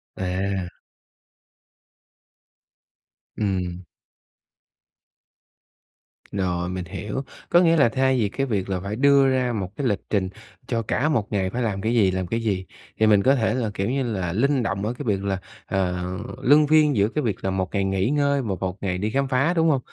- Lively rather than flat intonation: Yes, wide, 5.7 semitones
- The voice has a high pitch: No, low, 105 Hz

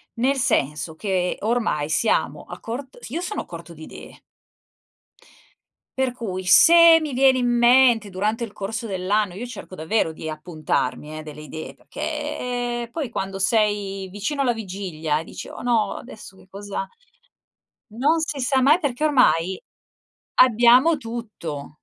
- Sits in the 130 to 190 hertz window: No, high, 220 Hz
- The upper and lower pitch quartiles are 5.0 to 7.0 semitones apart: Yes, wide, 5.5 semitones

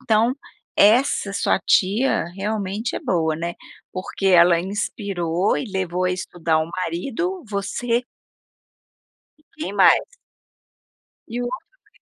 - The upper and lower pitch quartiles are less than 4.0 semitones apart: No, average, 4.3 semitones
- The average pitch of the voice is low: No, high, 195 Hz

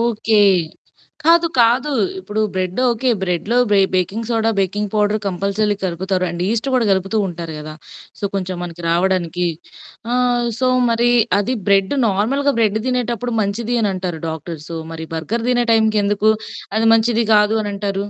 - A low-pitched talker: No, high, 210 Hz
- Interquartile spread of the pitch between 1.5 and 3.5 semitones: No, average, 4.0 semitones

